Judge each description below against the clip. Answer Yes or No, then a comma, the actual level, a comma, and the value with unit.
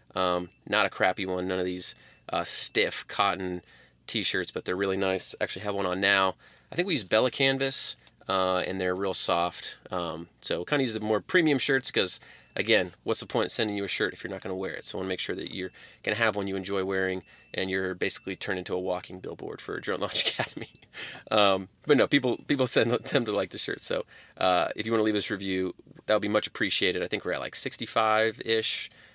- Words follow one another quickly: Yes, fast, 245 wpm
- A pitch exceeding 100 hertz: No, very low, 95 Hz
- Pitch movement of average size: Yes, average, 3.0 semitones